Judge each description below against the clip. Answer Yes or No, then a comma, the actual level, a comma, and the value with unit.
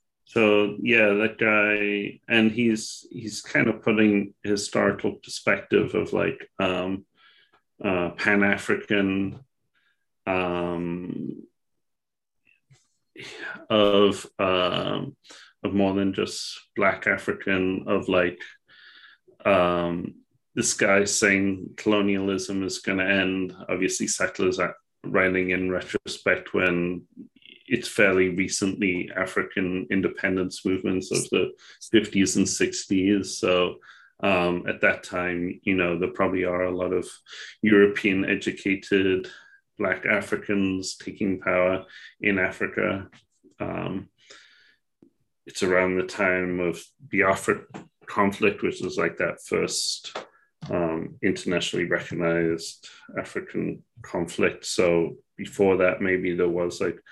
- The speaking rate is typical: No, slow, 105 wpm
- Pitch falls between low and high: No, very low, 95 Hz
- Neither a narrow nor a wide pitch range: No, narrow, 1.9 semitones